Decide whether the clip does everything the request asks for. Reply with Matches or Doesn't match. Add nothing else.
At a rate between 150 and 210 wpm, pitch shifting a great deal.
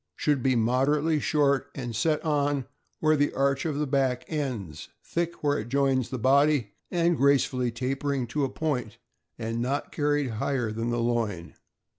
Doesn't match